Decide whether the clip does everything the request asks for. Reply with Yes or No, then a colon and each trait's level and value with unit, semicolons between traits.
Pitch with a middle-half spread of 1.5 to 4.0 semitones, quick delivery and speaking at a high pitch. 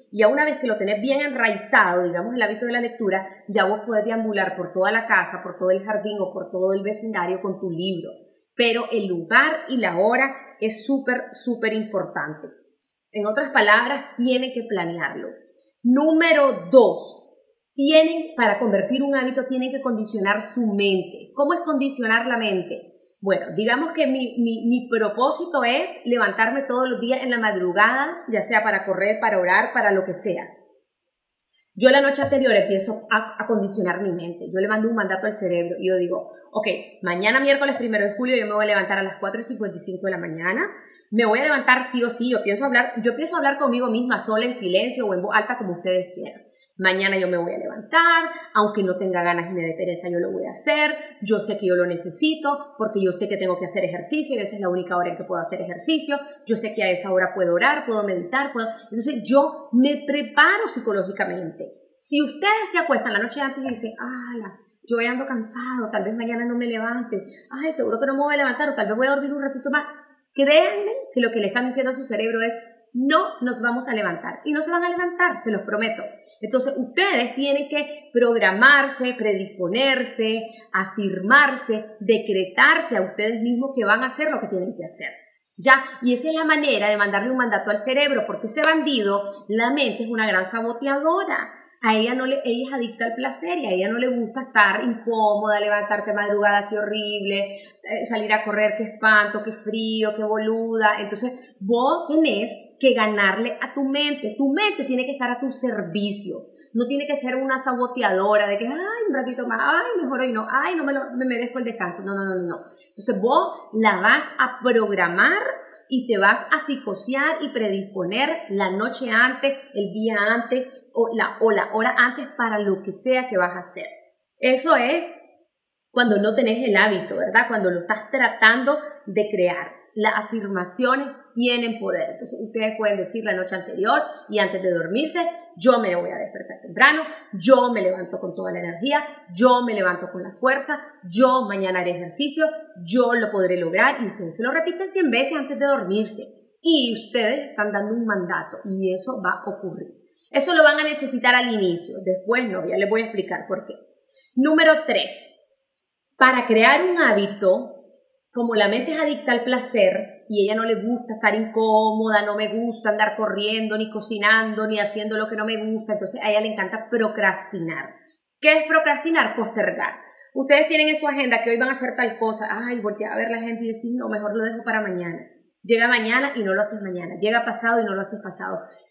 No: average, 4.8 semitones; fast, 200 wpm; high, 230 Hz